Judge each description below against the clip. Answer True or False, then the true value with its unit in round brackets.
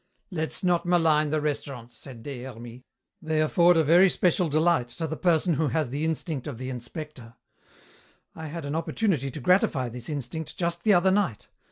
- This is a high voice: False (155 Hz)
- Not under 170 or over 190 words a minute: True (185 wpm)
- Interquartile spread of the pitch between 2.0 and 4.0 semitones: False (4.6 semitones)